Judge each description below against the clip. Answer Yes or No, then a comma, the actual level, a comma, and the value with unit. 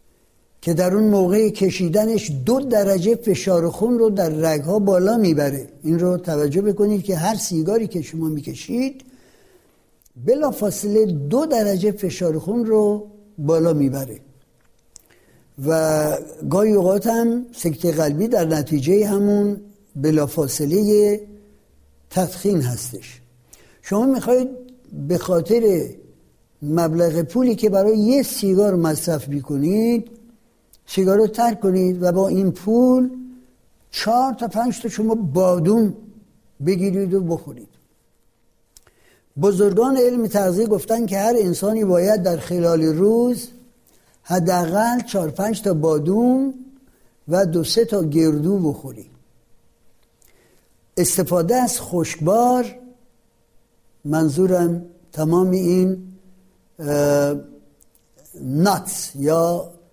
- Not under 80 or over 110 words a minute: Yes, slow, 105 wpm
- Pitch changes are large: No, average, 5.0 semitones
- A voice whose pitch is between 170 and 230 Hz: Yes, high, 190 Hz